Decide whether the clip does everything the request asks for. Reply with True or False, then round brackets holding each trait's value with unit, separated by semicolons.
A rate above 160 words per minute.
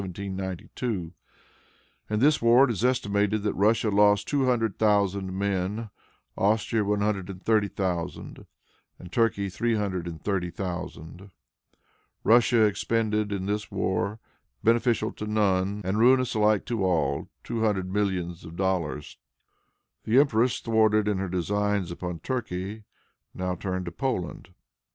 False (135 wpm)